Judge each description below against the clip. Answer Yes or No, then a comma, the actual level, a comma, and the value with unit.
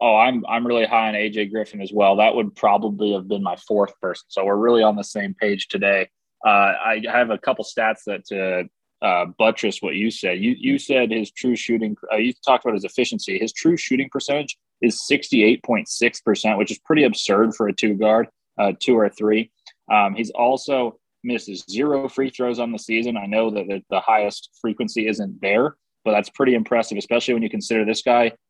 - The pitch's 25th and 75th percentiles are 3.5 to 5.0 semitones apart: No, average, 2.8 semitones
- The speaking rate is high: Yes, fast, 210 wpm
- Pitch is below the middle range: Yes, low, 110 Hz